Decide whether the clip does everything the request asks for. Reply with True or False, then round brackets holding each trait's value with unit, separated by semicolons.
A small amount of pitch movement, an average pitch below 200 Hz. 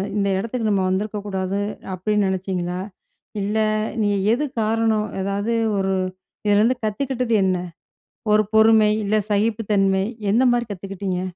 False (2.3 semitones; 205 Hz)